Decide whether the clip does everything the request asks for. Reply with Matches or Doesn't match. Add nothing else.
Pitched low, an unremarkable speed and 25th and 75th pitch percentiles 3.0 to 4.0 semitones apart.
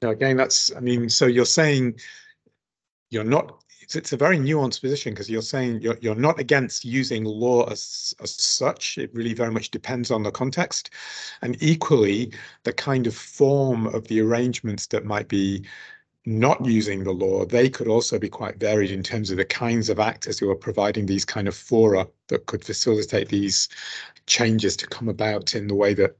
Matches